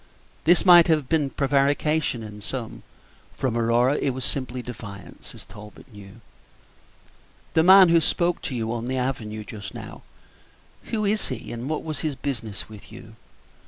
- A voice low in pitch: Yes, low, 130 Hz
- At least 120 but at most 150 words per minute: No, average, 160 wpm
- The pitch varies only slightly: No, wide, 5.6 semitones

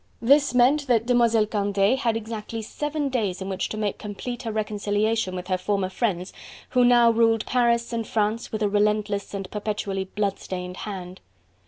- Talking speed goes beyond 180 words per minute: No, average, 170 wpm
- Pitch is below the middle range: No, high, 215 Hz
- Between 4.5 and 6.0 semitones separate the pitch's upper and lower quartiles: No, average, 2.8 semitones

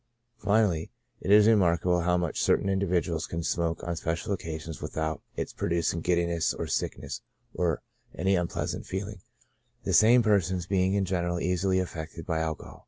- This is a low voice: Yes, very low, 90 Hz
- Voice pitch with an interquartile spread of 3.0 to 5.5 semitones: No, narrow, 2.5 semitones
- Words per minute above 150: Yes, average, 160 wpm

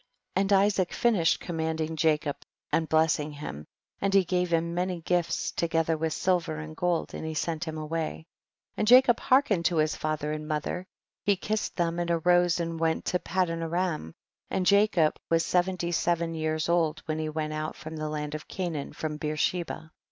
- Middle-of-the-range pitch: Yes, medium, 165 Hz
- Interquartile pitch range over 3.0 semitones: No, narrow, 2.4 semitones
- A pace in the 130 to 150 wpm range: No, average, 180 wpm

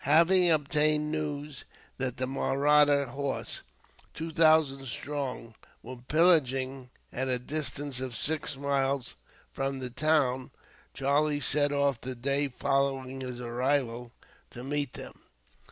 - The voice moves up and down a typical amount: No, narrow, 2.3 semitones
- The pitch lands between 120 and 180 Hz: Yes, medium, 140 Hz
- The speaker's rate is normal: No, slow, 120 wpm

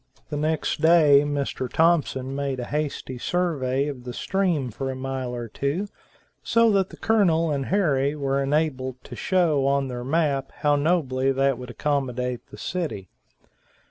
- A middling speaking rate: Yes, average, 160 wpm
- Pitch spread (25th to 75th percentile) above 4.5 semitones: No, average, 3.5 semitones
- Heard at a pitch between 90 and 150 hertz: Yes, medium, 140 Hz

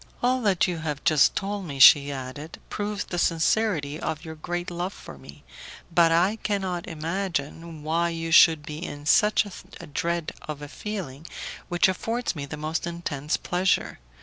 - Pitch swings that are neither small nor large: Yes, average, 3.7 semitones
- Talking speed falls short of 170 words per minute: Yes, average, 160 wpm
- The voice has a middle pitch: Yes, medium, 165 Hz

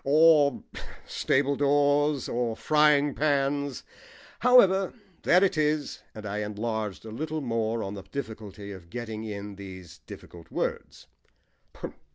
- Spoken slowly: Yes, slow, 125 wpm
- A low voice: Yes, low, 130 Hz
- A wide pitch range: Yes, wide, 5.8 semitones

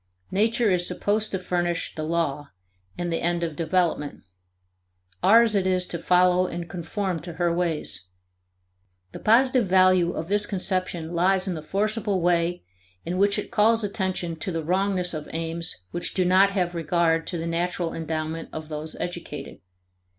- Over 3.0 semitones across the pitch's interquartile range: No, narrow, 2.4 semitones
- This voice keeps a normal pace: Yes, average, 165 wpm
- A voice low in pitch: No, medium, 175 Hz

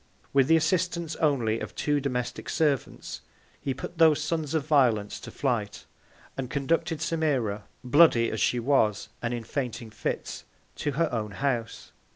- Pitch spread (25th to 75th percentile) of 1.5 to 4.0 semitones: No, average, 5.0 semitones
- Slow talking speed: No, average, 155 wpm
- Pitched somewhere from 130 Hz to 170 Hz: Yes, low, 135 Hz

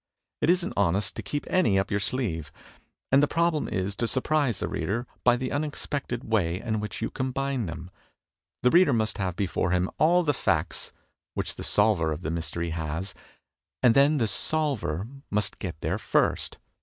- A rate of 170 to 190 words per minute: Yes, average, 180 wpm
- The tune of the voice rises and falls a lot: Yes, wide, 7.1 semitones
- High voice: No, low, 110 Hz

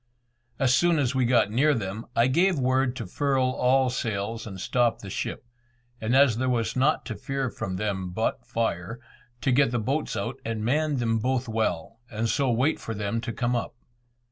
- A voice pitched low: Yes, low, 120 Hz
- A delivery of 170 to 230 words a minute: Yes, average, 195 wpm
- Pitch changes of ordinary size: Yes, average, 3.0 semitones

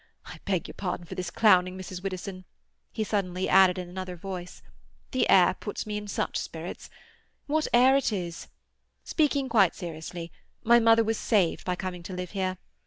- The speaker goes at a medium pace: Yes, average, 175 wpm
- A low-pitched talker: No, medium, 185 Hz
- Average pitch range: Yes, average, 3.2 semitones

